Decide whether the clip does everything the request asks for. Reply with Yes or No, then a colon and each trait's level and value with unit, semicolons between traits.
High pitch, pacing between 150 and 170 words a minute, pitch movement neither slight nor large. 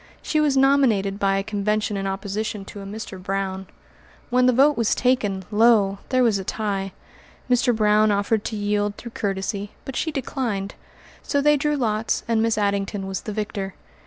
No: high, 210 Hz; average, 180 wpm; average, 3.4 semitones